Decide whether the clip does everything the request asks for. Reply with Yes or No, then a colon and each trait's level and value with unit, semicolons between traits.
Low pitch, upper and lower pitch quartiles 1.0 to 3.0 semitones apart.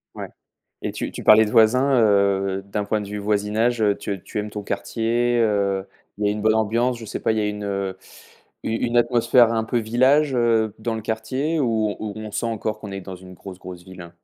Yes: low, 110 Hz; narrow, 2.5 semitones